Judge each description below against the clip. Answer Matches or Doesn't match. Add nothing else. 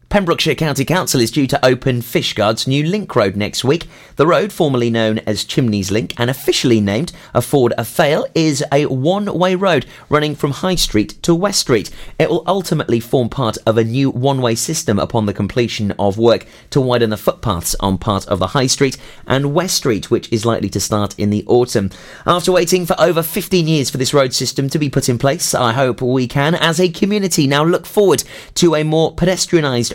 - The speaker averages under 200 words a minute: Doesn't match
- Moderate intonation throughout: Doesn't match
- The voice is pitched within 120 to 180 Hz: Matches